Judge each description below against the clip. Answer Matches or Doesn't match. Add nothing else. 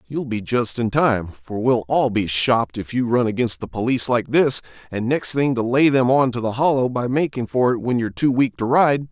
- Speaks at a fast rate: Matches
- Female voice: Doesn't match